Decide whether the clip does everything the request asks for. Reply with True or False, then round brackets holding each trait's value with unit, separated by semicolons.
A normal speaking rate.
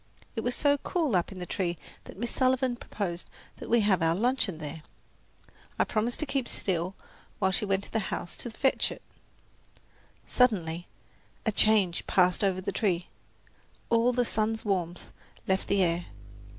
True (165 wpm)